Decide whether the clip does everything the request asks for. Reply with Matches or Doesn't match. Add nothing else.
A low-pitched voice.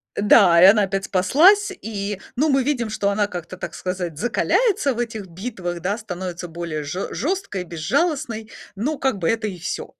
Doesn't match